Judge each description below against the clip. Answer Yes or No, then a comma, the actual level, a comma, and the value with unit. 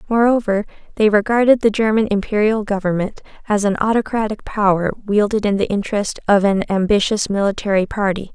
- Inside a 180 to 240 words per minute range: No, average, 145 wpm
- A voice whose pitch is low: No, high, 205 Hz